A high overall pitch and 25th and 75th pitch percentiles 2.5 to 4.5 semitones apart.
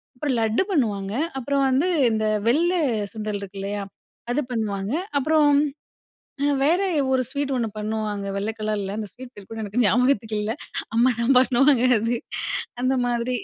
Yes: high, 235 Hz; average, 4.0 semitones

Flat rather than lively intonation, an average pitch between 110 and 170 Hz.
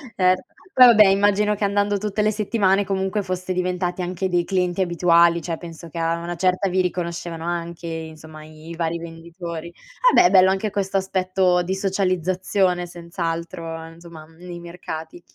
No: narrow, 2.2 semitones; medium, 180 Hz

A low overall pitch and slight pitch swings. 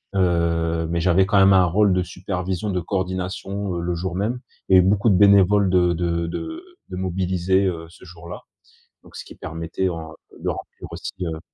Yes: very low, 90 Hz; narrow, 2.1 semitones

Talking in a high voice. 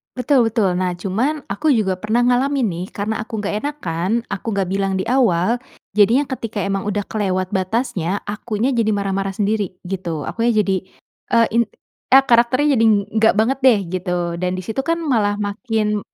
Yes: high, 210 Hz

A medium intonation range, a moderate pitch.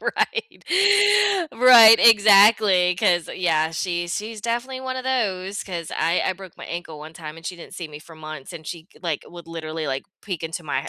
Yes: average, 4.8 semitones; medium, 175 Hz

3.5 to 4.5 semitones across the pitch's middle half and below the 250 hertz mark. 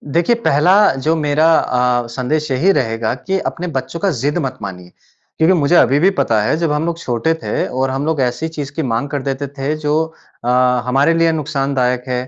Yes: average, 4.1 semitones; medium, 140 Hz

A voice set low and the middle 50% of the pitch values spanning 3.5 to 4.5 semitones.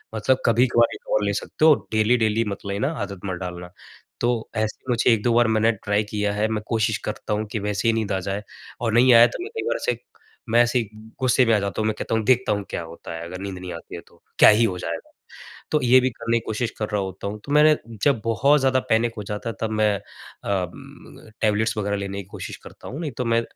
No: low, 110 Hz; average, 2.9 semitones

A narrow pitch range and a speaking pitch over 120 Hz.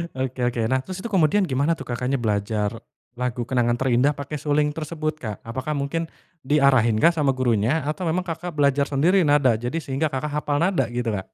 No: average, 3.9 semitones; medium, 140 Hz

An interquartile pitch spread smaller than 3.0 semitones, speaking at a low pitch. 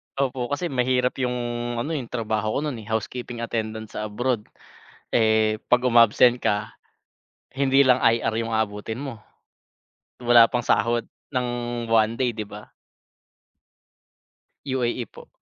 Yes: narrow, 2.4 semitones; low, 120 Hz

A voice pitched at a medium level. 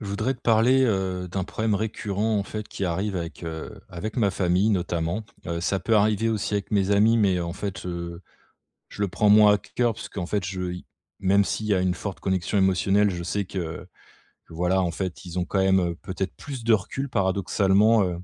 No: very low, 95 Hz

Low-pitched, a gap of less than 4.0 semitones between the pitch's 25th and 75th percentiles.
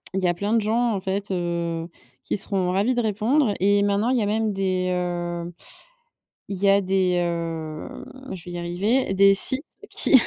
No: high, 195 Hz; average, 3.2 semitones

